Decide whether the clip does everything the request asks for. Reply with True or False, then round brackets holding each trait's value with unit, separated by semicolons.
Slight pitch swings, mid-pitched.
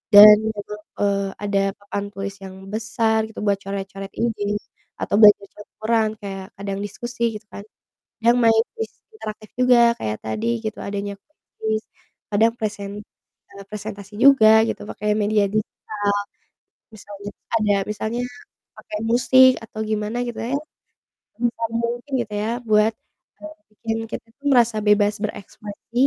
False (1.9 semitones; 215 Hz)